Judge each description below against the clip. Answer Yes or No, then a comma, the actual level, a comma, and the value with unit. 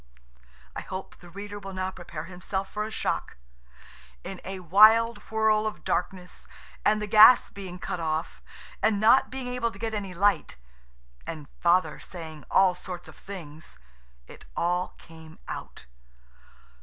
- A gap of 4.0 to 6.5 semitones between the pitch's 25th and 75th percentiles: No, average, 3.5 semitones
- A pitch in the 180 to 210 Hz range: Yes, high, 190 Hz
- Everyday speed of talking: Yes, average, 150 wpm